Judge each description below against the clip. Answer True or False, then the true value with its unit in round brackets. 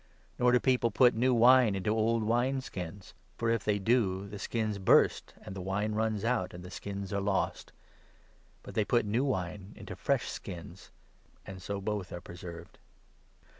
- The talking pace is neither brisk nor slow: True (180 wpm)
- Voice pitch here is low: True (105 Hz)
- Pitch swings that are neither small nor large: True (3.4 semitones)